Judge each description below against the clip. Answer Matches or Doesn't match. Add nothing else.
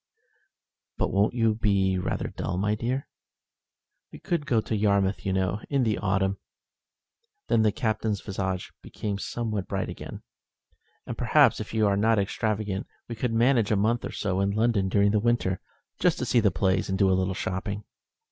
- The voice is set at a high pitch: Doesn't match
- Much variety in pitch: Doesn't match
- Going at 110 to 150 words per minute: Doesn't match